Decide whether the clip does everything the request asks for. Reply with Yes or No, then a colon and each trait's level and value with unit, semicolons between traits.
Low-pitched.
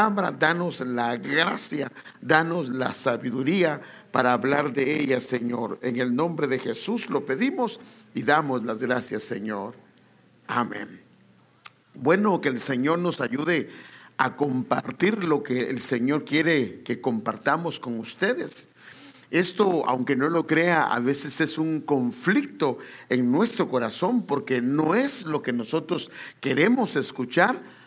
No: medium, 145 Hz